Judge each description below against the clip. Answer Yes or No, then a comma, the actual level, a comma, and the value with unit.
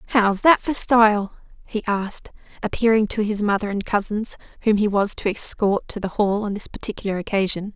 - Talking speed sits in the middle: Yes, average, 185 wpm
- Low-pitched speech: No, high, 210 Hz